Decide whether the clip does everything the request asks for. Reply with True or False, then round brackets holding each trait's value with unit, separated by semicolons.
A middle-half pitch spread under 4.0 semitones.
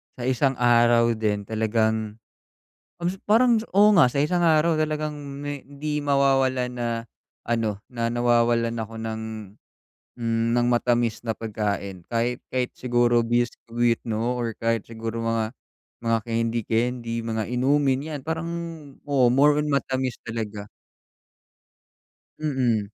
True (3.4 semitones)